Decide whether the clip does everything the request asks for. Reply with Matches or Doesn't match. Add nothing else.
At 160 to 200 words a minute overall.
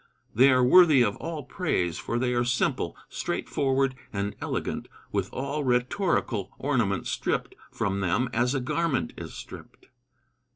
Doesn't match